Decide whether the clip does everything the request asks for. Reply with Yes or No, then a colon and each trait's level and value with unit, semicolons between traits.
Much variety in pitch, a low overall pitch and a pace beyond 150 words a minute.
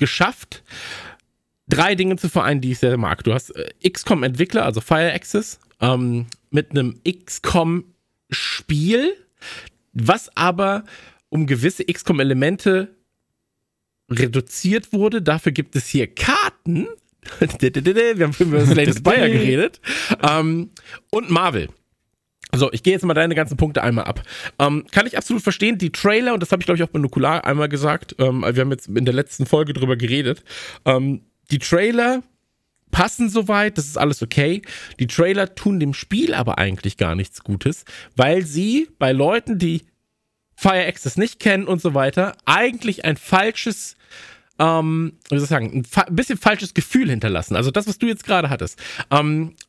No: wide, 6.2 semitones; medium, 160 Hz; average, 160 wpm